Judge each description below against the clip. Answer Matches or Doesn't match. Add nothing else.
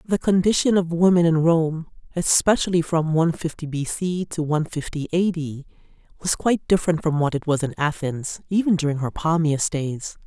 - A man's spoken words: Doesn't match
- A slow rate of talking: Doesn't match